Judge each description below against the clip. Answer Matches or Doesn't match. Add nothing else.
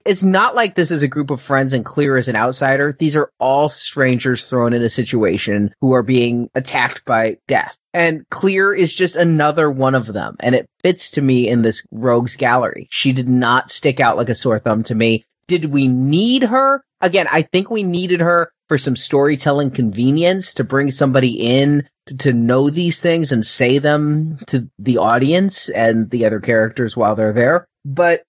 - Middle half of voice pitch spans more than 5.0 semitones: Matches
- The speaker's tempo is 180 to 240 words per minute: Matches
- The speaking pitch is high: Doesn't match